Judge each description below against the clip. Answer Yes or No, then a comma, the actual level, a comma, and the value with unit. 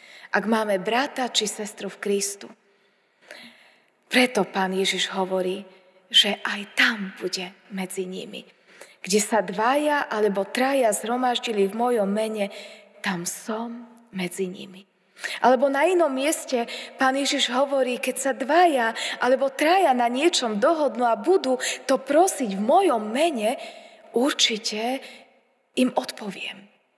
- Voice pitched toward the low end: No, high, 235 Hz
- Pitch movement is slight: No, average, 5.0 semitones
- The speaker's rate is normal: Yes, average, 120 wpm